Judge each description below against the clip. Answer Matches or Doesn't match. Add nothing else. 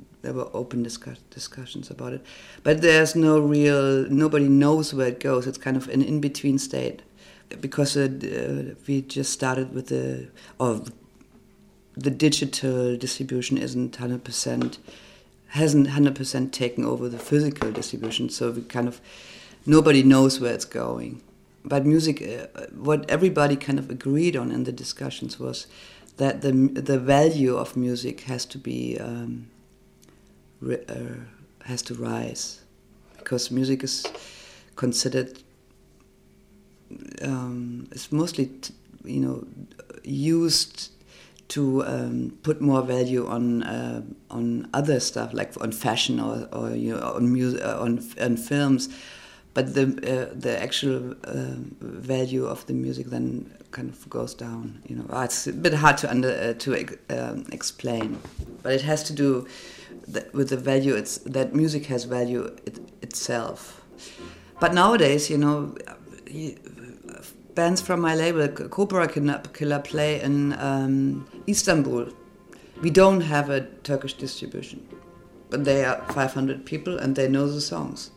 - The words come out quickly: Doesn't match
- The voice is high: Doesn't match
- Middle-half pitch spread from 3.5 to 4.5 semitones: Doesn't match